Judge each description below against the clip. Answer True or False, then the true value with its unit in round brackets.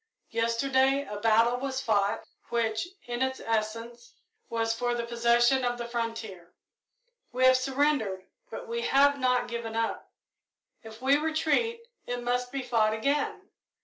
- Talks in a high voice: True (240 Hz)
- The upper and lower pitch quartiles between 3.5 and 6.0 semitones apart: False (2.8 semitones)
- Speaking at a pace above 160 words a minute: False (145 wpm)